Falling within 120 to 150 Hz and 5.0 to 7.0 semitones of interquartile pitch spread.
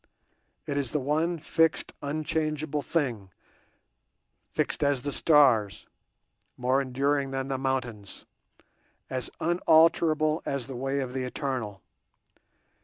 No: medium, 140 Hz; average, 3.0 semitones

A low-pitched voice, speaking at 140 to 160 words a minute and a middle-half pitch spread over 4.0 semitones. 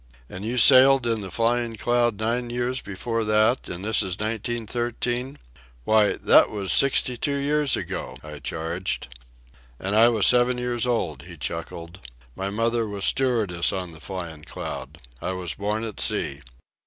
Yes: low, 110 Hz; average, 155 wpm; average, 4.7 semitones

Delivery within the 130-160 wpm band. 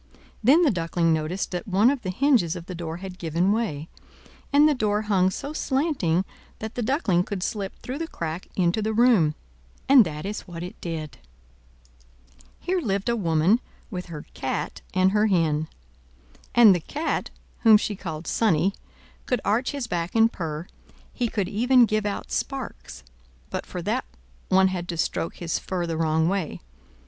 No: average, 175 wpm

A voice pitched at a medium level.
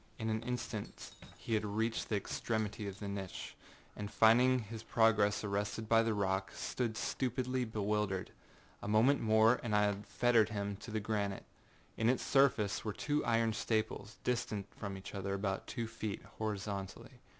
No: low, 110 Hz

